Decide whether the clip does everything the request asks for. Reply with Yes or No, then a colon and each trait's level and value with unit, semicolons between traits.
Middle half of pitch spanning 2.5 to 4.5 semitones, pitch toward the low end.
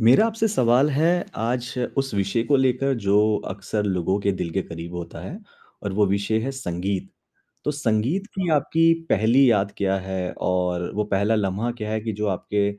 No: wide, 5.5 semitones; low, 105 Hz